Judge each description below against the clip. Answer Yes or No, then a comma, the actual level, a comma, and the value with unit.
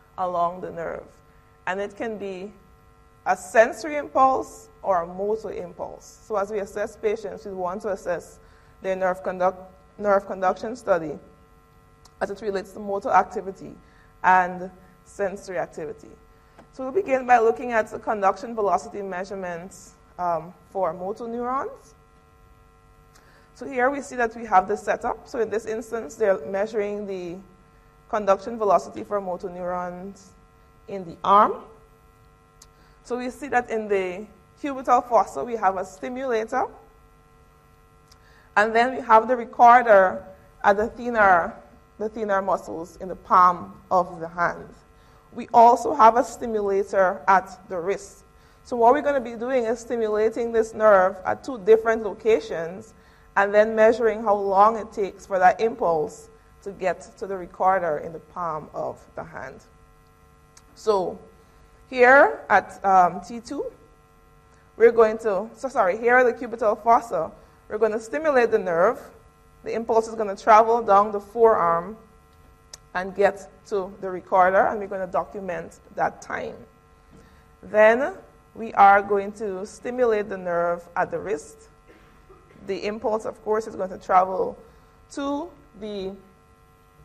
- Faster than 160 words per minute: No, average, 145 wpm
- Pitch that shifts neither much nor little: Yes, average, 3.7 semitones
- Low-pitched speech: No, high, 205 Hz